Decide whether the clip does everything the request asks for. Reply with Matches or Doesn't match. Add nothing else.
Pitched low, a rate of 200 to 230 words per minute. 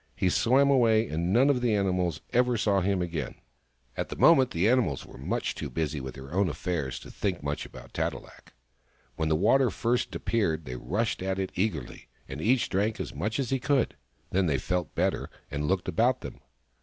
Matches